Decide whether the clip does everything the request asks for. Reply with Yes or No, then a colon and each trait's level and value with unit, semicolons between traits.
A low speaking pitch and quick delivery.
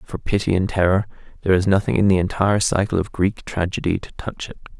Yes: very low, 95 Hz; fast, 215 wpm